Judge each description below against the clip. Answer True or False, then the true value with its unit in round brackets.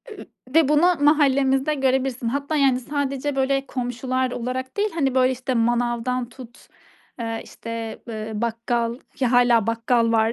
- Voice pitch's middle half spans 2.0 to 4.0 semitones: True (2.7 semitones)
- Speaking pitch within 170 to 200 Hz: False (255 Hz)